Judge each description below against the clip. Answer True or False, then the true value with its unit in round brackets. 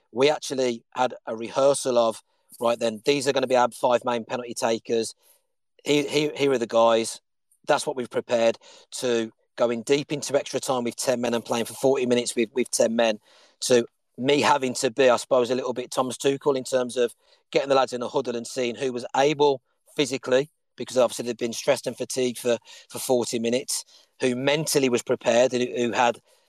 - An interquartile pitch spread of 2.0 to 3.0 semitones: True (2.5 semitones)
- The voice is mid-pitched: False (125 Hz)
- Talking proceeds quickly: True (210 wpm)